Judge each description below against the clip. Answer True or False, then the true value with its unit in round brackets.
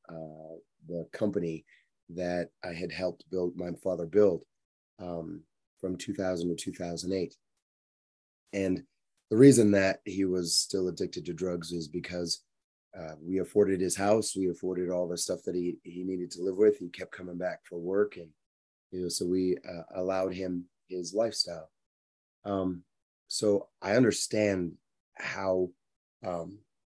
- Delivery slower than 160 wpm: True (150 wpm)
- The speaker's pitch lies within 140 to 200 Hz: False (90 Hz)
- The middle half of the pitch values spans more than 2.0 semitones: False (1.5 semitones)